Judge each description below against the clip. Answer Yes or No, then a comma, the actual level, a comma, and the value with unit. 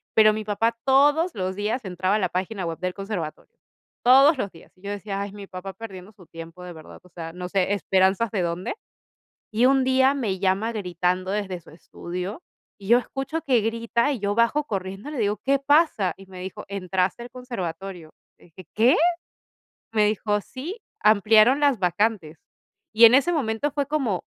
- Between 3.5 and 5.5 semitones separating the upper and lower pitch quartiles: Yes, average, 4.8 semitones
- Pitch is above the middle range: Yes, high, 205 Hz